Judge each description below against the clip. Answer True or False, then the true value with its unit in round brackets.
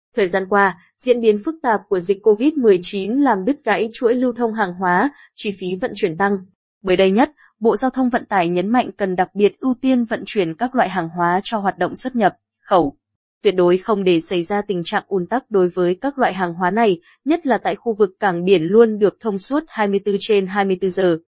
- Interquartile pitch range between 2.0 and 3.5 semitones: False (4.1 semitones)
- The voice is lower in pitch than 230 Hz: True (205 Hz)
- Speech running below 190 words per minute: False (230 wpm)